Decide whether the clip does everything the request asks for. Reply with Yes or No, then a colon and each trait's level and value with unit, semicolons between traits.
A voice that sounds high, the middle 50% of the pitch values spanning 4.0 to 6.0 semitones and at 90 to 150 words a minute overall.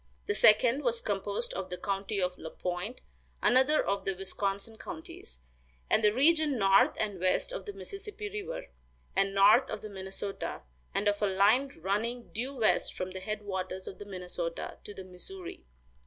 No: high, 205 Hz; average, 4.7 semitones; average, 175 wpm